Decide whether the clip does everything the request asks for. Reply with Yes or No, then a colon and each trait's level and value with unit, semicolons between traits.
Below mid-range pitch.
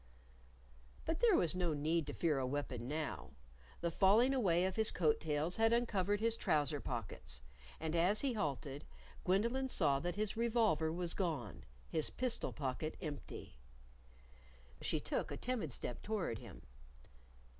No: medium, 170 Hz